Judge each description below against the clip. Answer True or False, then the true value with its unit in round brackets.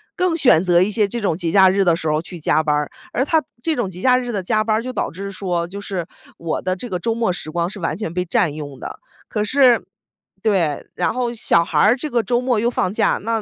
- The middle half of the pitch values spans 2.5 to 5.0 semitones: False (5.6 semitones)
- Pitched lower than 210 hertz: True (195 Hz)